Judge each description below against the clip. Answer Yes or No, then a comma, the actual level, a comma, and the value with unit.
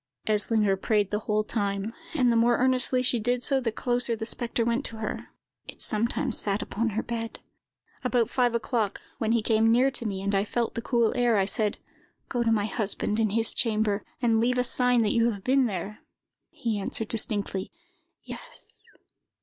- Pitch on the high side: Yes, high, 225 Hz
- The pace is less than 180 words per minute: No, average, 190 wpm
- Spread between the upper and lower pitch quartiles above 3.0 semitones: No, narrow, 2.4 semitones